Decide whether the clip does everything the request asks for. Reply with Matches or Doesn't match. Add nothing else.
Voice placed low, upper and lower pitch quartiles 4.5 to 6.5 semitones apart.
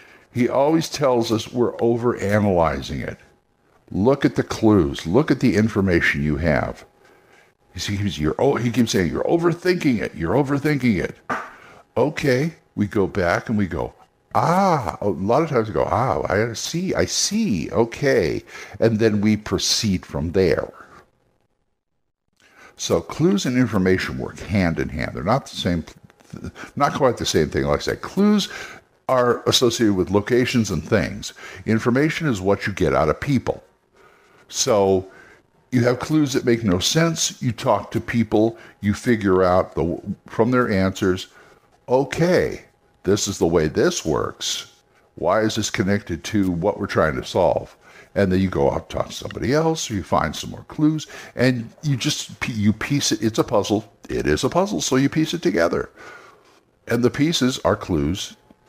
Matches